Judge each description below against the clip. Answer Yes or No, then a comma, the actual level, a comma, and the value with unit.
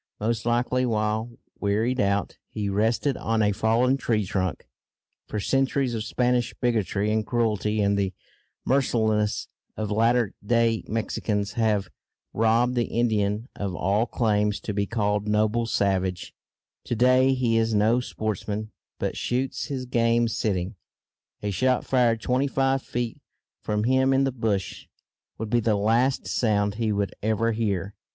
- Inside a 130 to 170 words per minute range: Yes, average, 145 wpm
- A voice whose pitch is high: No, low, 110 Hz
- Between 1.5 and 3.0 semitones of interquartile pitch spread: Yes, average, 2.7 semitones